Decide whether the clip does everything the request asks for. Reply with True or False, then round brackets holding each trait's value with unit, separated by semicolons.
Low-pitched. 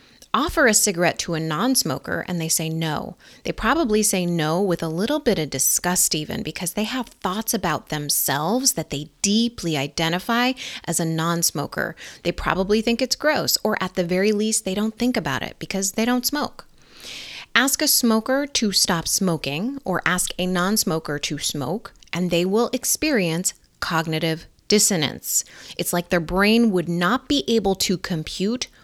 False (190 Hz)